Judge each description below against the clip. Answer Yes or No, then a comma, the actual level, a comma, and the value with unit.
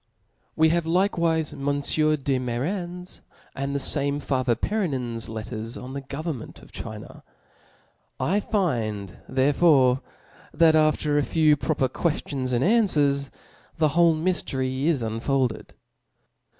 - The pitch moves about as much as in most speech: Yes, average, 4.0 semitones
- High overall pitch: No, medium, 145 Hz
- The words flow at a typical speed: No, slow, 125 wpm